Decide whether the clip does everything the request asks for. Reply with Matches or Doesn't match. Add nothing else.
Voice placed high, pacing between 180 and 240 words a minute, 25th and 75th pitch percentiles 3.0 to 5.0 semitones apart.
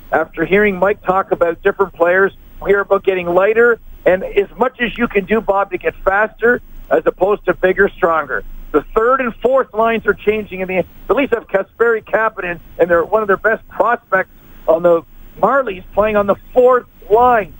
Matches